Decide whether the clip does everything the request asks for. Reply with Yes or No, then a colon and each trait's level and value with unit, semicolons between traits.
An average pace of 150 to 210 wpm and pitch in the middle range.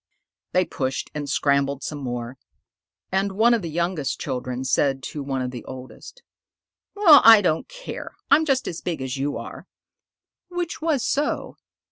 Yes: average, 160 wpm; medium, 155 Hz